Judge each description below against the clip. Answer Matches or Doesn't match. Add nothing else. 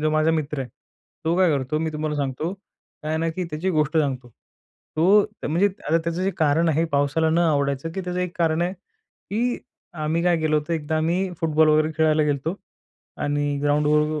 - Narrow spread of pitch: Matches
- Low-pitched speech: Doesn't match